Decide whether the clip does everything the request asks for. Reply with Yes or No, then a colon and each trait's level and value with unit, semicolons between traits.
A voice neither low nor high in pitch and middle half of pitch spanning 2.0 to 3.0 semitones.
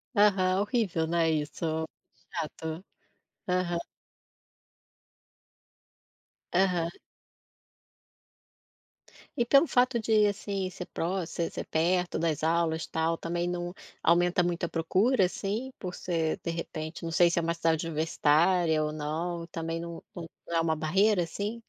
Yes: medium, 170 Hz; narrow, 2.4 semitones